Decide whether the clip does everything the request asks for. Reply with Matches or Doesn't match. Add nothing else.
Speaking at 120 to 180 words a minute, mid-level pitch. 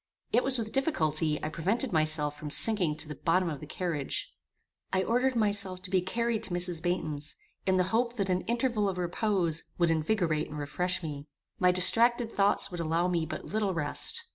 Doesn't match